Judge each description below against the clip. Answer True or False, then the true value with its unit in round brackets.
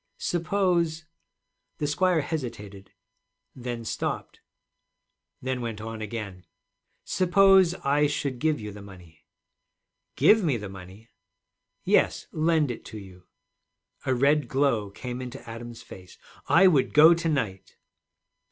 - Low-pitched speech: True (130 Hz)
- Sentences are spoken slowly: True (125 wpm)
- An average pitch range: False (7.0 semitones)